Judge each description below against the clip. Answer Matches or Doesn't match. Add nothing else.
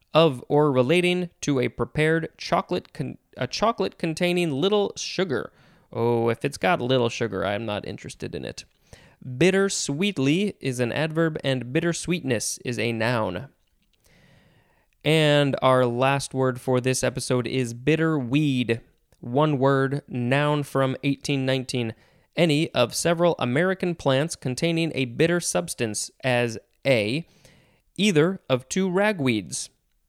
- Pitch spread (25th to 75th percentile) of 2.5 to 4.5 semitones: Doesn't match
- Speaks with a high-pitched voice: Doesn't match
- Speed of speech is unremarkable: Doesn't match